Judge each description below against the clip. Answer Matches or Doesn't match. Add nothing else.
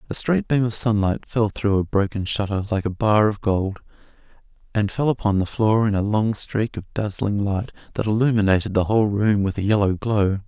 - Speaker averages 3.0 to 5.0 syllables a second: Doesn't match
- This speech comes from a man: Matches